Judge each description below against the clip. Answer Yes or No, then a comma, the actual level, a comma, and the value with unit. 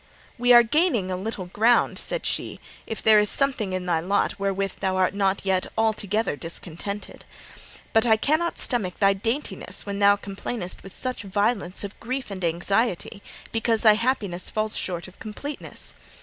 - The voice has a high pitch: Yes, high, 205 Hz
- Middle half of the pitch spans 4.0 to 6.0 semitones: No, average, 3.3 semitones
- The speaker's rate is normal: Yes, average, 165 wpm